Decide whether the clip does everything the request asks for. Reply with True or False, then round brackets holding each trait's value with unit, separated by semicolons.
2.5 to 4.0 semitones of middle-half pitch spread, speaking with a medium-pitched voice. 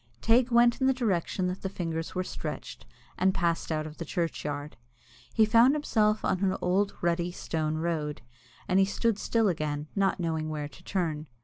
False (5.0 semitones; 180 Hz)